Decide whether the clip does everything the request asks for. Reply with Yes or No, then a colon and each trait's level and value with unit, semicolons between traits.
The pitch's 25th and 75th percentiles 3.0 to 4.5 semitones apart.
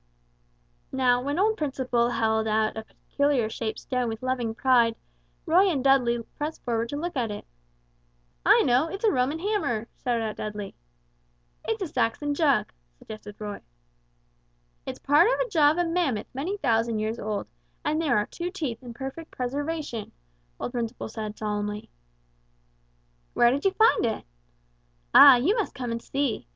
No: average, 5.3 semitones